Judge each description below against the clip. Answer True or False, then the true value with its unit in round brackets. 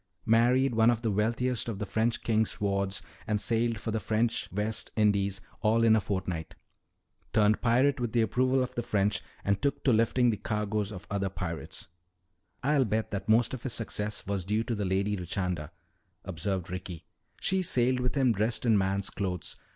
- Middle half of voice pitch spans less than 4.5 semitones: True (3.1 semitones)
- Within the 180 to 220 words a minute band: True (185 wpm)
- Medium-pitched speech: False (110 Hz)